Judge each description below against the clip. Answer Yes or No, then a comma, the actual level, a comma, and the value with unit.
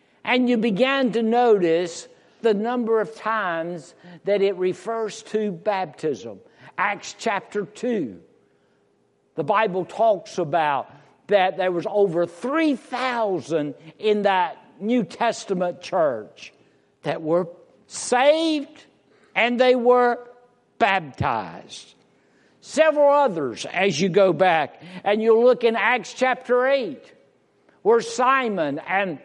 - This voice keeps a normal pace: No, slow, 110 wpm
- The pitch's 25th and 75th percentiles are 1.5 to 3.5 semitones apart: No, average, 5.1 semitones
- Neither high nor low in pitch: No, high, 220 Hz